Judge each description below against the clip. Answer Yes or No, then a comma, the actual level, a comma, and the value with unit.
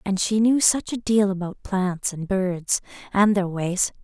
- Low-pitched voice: No, high, 195 Hz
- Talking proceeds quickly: No, average, 195 wpm